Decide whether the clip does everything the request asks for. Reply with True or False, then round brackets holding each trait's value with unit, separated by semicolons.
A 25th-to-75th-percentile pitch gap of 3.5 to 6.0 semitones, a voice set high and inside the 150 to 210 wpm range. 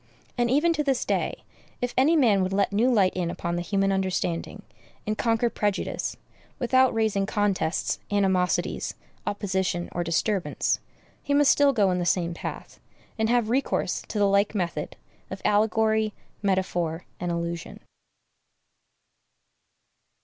False (3.9 semitones; 200 Hz; 140 wpm)